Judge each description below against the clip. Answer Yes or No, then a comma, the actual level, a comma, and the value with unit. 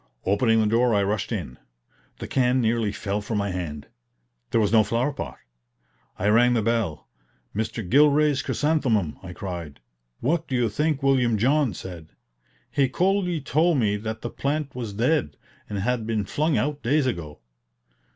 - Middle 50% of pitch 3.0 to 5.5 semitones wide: Yes, average, 5.2 semitones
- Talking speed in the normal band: Yes, average, 165 wpm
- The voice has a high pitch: No, low, 115 Hz